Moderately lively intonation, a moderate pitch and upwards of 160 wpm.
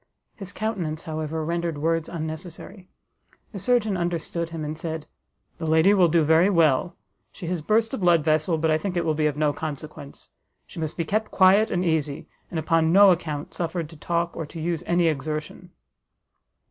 No: narrow, 2.3 semitones; medium, 165 Hz; average, 185 wpm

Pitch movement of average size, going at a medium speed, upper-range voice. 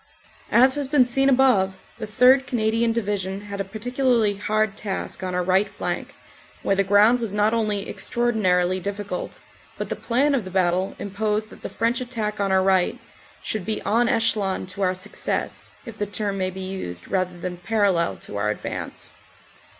Yes: average, 3.4 semitones; average, 180 wpm; high, 205 Hz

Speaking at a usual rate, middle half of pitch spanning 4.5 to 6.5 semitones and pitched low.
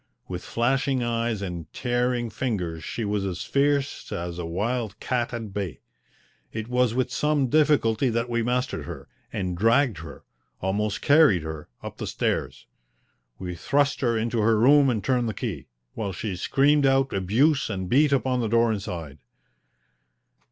Yes: average, 160 wpm; average, 5.1 semitones; low, 115 Hz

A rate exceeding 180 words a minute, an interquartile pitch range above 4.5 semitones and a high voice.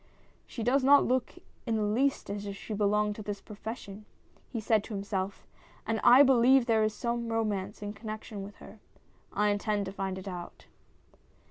No: average, 195 wpm; narrow, 2.4 semitones; high, 215 Hz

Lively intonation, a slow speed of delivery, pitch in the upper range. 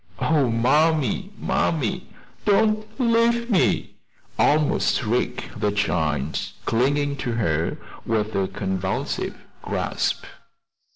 No: wide, 7.9 semitones; slow, 95 wpm; low, 125 Hz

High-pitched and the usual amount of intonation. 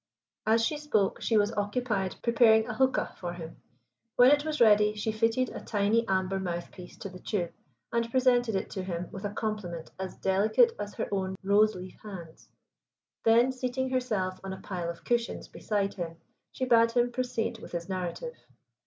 Yes: high, 215 Hz; average, 4.1 semitones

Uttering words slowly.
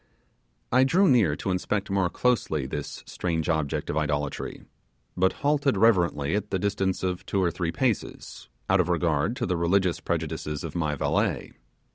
No: average, 165 wpm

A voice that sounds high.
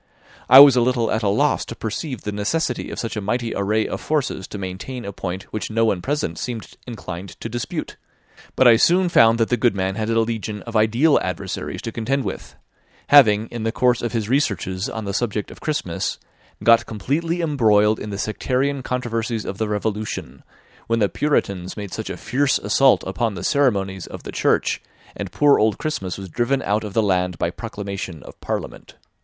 No: low, 110 Hz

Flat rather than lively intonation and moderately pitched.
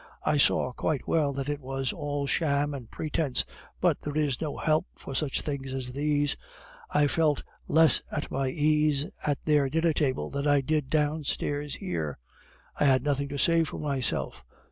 Yes: narrow, 1.9 semitones; medium, 145 Hz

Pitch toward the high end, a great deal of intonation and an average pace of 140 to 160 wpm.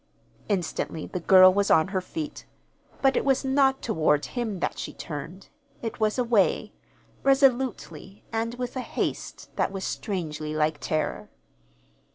Yes: high, 200 Hz; wide, 7.5 semitones; average, 145 wpm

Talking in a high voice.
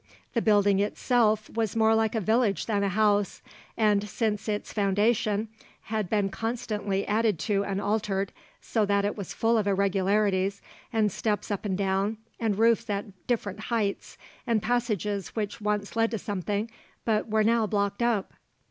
Yes: high, 210 Hz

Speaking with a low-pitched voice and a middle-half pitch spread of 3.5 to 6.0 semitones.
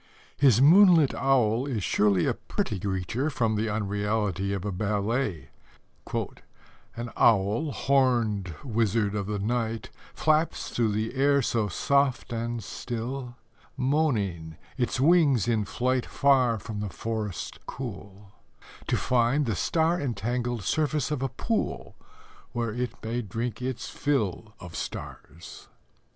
Yes: low, 115 Hz; average, 4.4 semitones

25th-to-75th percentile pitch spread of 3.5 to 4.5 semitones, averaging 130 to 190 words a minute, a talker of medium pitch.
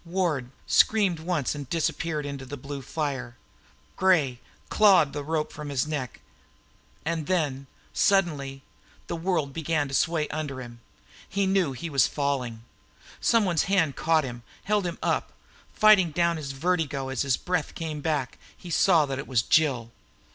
Yes: average, 3.9 semitones; average, 160 wpm; medium, 150 Hz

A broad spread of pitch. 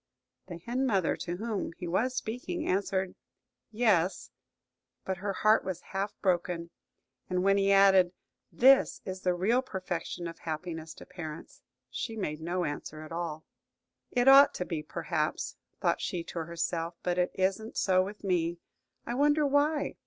No: average, 4.2 semitones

